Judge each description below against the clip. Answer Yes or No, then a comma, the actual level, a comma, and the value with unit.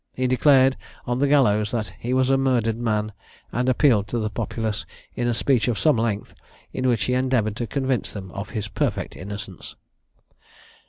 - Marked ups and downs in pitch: No, average, 3.4 semitones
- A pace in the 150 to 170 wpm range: No, average, 180 wpm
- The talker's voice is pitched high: No, low, 120 Hz